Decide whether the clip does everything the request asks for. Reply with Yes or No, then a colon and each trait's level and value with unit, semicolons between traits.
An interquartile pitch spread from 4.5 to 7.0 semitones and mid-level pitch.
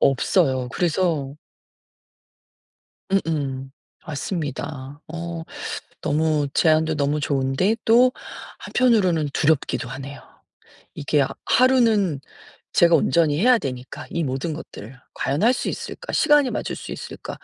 Yes: average, 5.2 semitones; medium, 155 Hz